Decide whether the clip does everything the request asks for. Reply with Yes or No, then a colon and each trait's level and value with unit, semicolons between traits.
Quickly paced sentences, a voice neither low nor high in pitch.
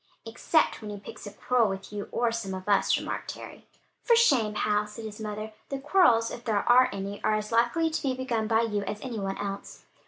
No: fast, 225 wpm; high, 220 Hz